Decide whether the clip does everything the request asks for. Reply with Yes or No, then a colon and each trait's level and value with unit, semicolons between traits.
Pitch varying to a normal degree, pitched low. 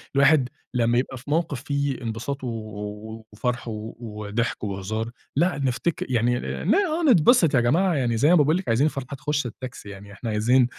Yes: average, 4.4 semitones; low, 125 Hz